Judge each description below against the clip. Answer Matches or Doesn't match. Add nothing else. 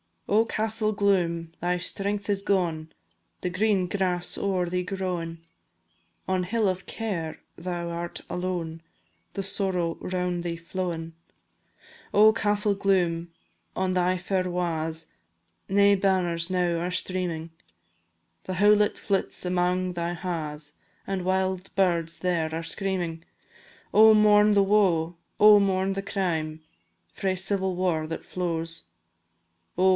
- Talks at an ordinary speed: Doesn't match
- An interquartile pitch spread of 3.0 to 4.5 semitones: Doesn't match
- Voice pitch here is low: Doesn't match